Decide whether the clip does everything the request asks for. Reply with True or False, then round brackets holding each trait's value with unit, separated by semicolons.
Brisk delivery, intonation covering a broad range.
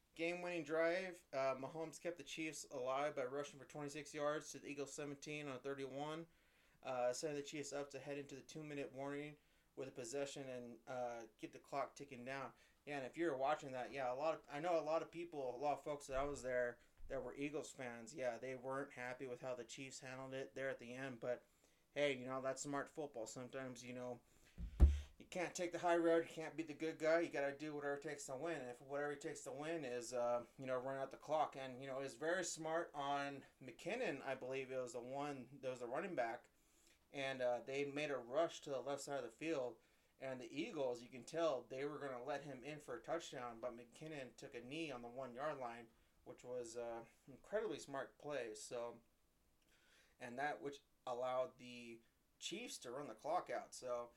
False (230 wpm; 3.2 semitones)